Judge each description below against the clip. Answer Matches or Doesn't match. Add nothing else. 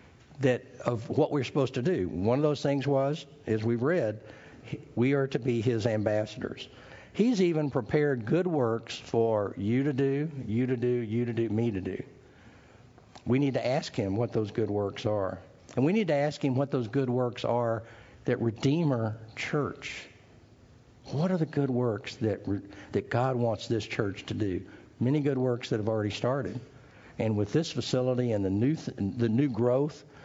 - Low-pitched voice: Matches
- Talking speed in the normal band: Matches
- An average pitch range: Matches